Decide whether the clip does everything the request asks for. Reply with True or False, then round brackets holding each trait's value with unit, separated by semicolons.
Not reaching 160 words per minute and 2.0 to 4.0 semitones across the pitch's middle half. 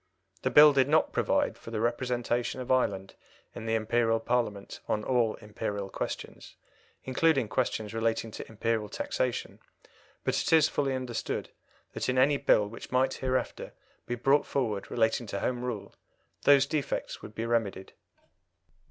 True (150 wpm; 2.8 semitones)